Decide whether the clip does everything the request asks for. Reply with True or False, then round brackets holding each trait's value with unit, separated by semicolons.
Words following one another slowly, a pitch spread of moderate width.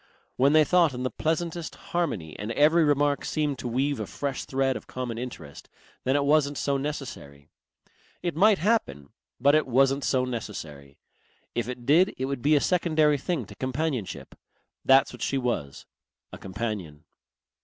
False (165 wpm; 4.4 semitones)